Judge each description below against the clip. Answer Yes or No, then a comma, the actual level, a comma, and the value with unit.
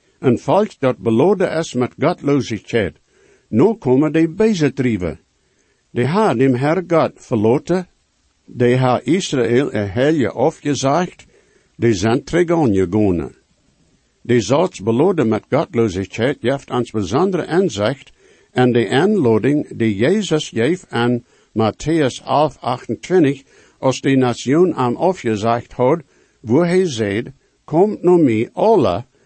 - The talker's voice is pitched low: Yes, low, 130 Hz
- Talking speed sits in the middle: No, slow, 120 wpm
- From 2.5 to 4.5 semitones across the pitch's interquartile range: No, wide, 5.6 semitones